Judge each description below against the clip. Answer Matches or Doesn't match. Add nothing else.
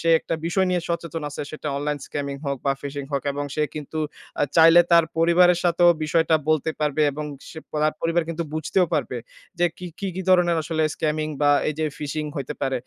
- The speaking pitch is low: Doesn't match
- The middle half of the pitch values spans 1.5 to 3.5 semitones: Matches